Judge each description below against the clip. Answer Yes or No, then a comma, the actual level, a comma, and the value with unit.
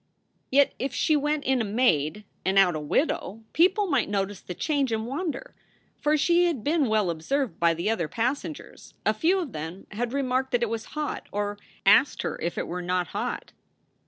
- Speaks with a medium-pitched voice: No, high, 235 Hz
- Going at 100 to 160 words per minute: No, average, 195 wpm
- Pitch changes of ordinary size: No, wide, 6.8 semitones